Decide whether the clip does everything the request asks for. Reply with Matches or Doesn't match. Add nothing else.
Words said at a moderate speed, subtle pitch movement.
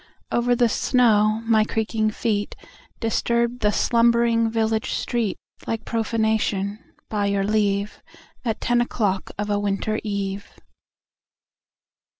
Doesn't match